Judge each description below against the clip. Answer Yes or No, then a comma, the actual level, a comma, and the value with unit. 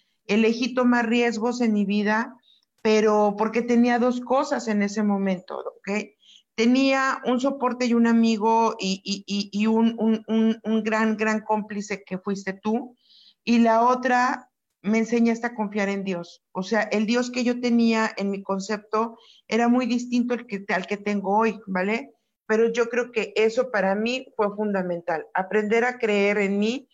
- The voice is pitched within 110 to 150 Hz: No, high, 220 Hz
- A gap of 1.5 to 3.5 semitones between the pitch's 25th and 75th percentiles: Yes, narrow, 2.5 semitones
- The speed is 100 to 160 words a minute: No, average, 175 wpm